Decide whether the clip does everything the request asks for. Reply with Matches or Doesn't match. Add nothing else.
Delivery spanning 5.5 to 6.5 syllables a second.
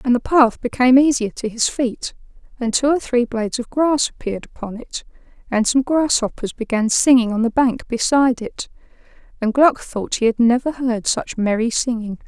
Doesn't match